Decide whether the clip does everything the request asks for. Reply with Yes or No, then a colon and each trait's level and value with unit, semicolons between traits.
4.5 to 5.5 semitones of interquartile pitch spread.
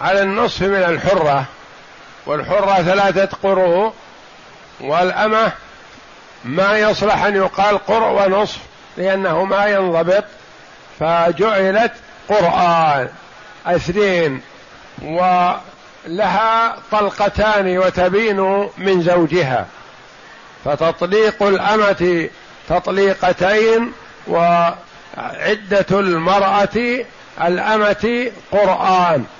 No: average, 2.7 semitones